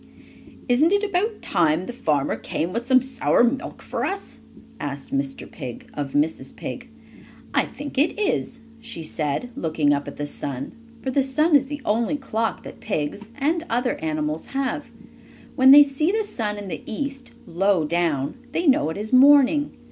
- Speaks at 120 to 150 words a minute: No, average, 175 wpm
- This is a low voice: No, high, 235 Hz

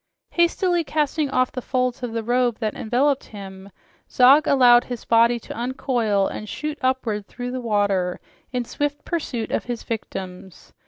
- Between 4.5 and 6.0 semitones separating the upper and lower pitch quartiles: No, average, 3.7 semitones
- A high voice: Yes, high, 245 Hz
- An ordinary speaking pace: Yes, average, 160 wpm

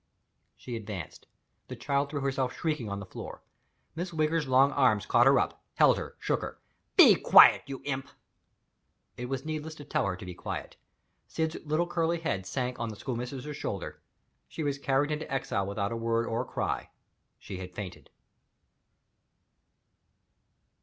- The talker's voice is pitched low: Yes, low, 130 Hz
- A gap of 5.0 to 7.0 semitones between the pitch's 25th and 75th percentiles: Yes, wide, 5.6 semitones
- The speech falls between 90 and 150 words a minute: No, average, 165 wpm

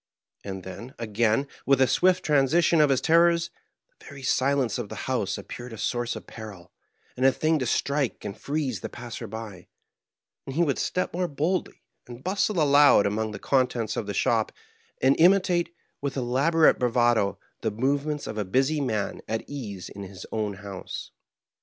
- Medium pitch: No, low, 130 Hz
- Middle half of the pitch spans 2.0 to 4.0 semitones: No, wide, 5.4 semitones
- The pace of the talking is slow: No, average, 175 wpm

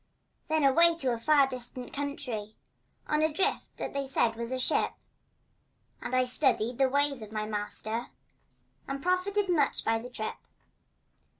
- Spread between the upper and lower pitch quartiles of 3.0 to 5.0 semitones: Yes, average, 4.2 semitones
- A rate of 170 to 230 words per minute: No, average, 160 wpm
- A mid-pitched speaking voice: No, very high, 260 Hz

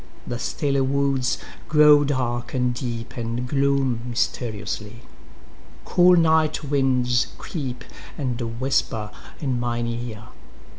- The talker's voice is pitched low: Yes, low, 125 Hz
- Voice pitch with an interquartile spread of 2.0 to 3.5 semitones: Yes, average, 2.8 semitones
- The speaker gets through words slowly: Yes, slow, 95 wpm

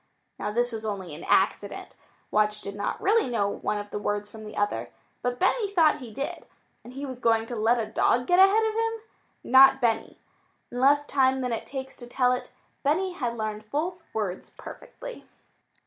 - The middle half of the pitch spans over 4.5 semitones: Yes, average, 5.3 semitones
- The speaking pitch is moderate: No, high, 245 Hz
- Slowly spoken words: No, average, 195 wpm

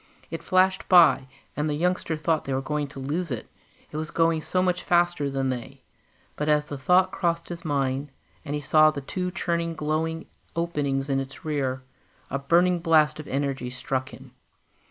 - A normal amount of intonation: Yes, average, 3.5 semitones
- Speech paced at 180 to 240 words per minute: Yes, average, 185 wpm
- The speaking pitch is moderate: Yes, medium, 155 Hz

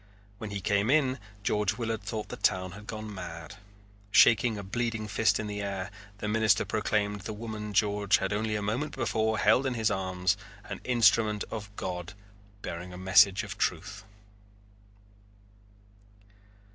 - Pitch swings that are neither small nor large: No, narrow, 2.3 semitones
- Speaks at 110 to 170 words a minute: Yes, average, 155 wpm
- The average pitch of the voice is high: No, low, 105 Hz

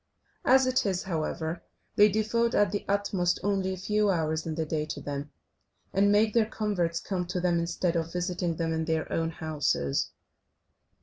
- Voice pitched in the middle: Yes, medium, 180 Hz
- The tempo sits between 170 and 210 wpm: Yes, average, 180 wpm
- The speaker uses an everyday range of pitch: Yes, average, 3.9 semitones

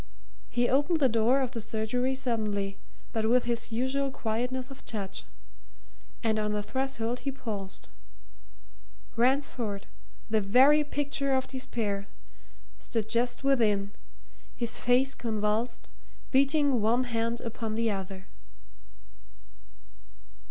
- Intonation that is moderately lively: Yes, average, 3.4 semitones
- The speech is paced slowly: Yes, slow, 115 wpm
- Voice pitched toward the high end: Yes, high, 235 Hz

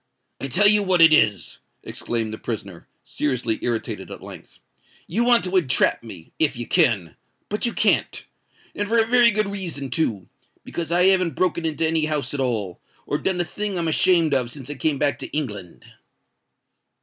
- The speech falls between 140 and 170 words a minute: No, average, 180 wpm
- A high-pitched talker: No, medium, 155 Hz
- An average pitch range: No, wide, 7.6 semitones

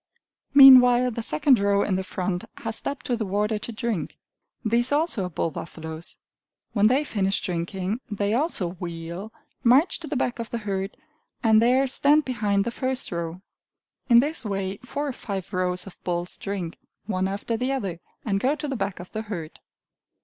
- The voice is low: No, high, 210 Hz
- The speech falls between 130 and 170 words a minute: No, average, 185 wpm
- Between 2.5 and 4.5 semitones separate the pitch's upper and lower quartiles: No, average, 5.0 semitones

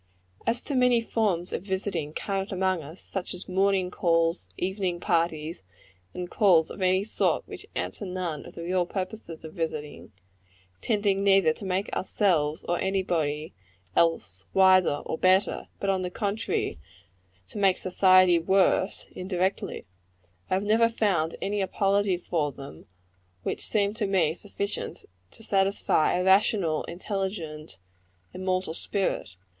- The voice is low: No, medium, 185 Hz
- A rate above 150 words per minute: No, average, 140 wpm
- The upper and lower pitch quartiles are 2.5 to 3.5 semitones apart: Yes, average, 2.9 semitones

